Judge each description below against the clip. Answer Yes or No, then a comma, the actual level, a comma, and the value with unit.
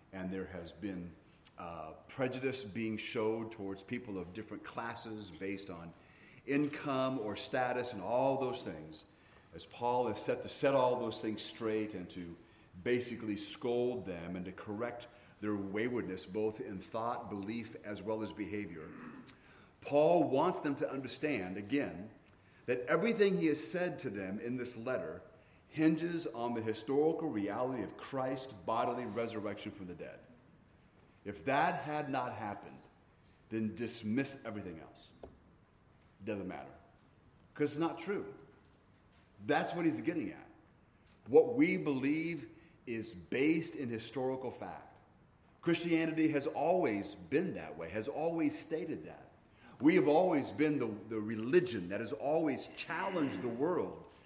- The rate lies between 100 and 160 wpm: Yes, average, 145 wpm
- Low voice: Yes, low, 115 Hz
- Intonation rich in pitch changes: Yes, wide, 5.7 semitones